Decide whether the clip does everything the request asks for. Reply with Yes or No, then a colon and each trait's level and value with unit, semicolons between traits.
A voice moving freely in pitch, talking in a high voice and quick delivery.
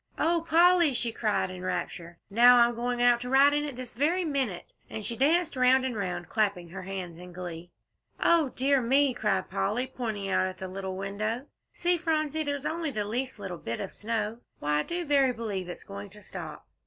Yes: wide, 6.3 semitones; high, 235 Hz; fast, 210 wpm